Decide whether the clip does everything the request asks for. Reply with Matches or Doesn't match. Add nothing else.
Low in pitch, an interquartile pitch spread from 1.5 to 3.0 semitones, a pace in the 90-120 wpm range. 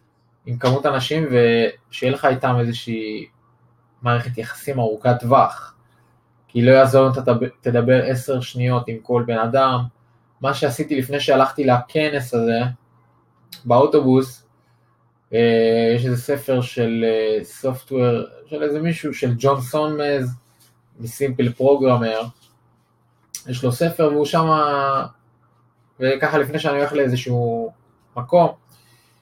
Matches